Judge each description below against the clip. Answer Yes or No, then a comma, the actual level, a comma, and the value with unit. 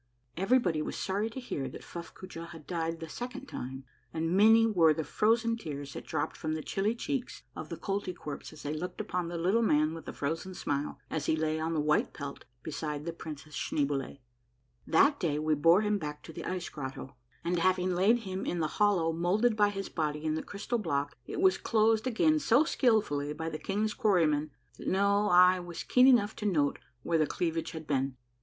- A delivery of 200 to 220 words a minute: Yes, fast, 205 wpm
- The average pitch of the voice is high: No, medium, 170 Hz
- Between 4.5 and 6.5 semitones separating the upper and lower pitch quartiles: Yes, average, 5.2 semitones